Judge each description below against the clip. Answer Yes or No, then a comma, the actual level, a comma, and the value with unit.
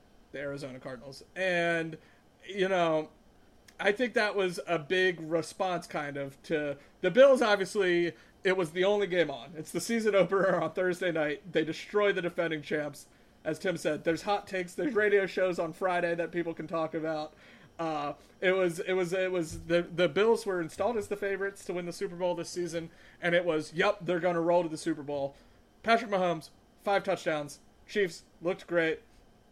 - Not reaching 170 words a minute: No, average, 190 wpm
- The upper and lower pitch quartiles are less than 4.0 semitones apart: Yes, average, 3.0 semitones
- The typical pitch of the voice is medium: Yes, medium, 175 Hz